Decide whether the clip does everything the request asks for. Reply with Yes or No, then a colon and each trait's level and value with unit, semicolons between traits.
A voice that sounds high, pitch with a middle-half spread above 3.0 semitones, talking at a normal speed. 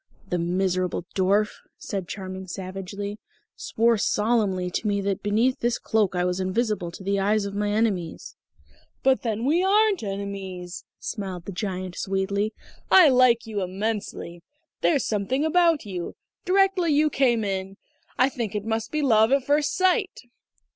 Yes: high, 205 Hz; average, 4.6 semitones; average, 155 wpm